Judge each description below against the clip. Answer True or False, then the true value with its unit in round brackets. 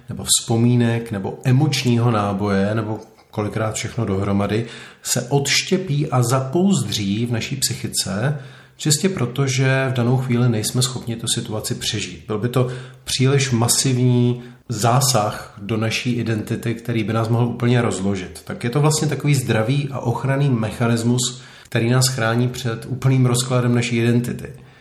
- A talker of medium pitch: False (120 Hz)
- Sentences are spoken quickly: False (145 wpm)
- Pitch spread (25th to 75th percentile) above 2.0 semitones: True (2.5 semitones)